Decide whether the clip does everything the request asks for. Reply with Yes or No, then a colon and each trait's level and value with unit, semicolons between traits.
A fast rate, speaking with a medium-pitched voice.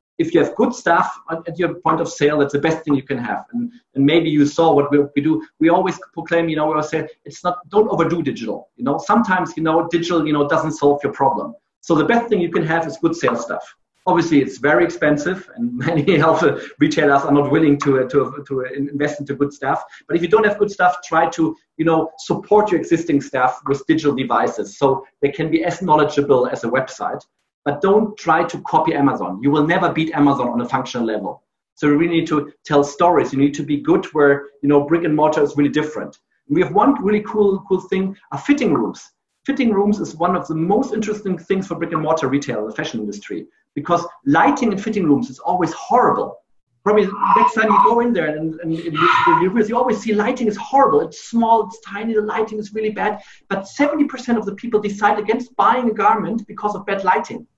Yes: fast, 230 wpm; medium, 165 Hz